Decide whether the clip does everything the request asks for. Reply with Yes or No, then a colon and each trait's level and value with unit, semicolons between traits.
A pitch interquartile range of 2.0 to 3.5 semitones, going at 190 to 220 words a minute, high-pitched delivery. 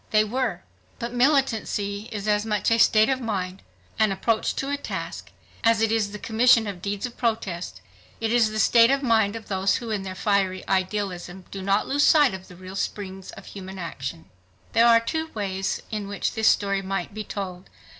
Yes: average, 3.0 semitones; average, 200 wpm; high, 210 Hz